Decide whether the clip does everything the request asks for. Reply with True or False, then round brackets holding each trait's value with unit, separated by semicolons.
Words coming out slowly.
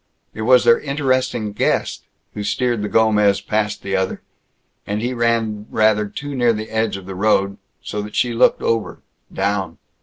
False (175 wpm)